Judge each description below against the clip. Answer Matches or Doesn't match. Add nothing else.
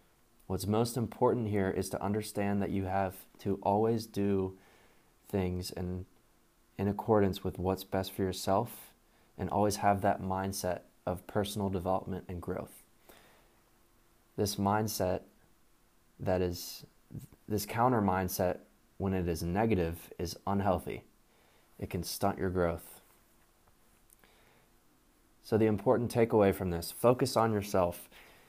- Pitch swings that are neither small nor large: Doesn't match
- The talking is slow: Matches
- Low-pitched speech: Matches